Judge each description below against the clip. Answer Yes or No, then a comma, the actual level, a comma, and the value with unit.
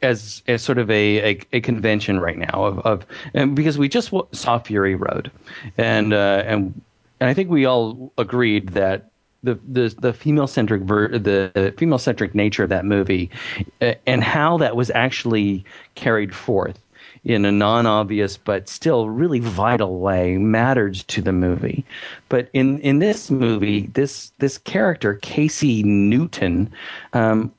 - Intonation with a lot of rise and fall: No, average, 4.2 semitones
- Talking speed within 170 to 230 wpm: No, average, 155 wpm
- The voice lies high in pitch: No, low, 110 Hz